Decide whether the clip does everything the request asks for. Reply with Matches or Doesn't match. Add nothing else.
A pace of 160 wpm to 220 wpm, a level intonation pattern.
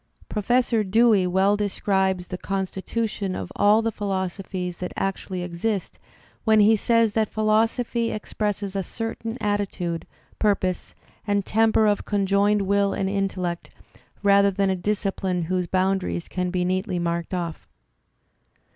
Doesn't match